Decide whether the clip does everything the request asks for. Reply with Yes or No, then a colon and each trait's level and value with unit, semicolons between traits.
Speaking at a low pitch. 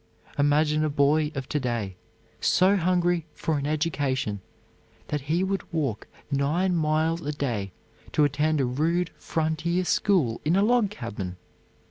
No: medium, 155 Hz